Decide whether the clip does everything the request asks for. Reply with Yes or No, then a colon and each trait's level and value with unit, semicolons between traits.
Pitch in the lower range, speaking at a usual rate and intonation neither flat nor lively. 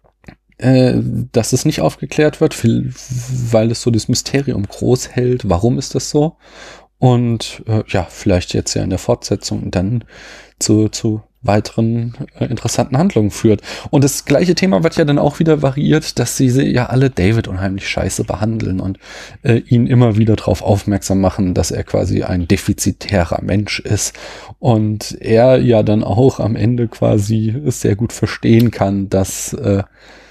Yes: low, 115 Hz; average, 160 wpm; average, 3.9 semitones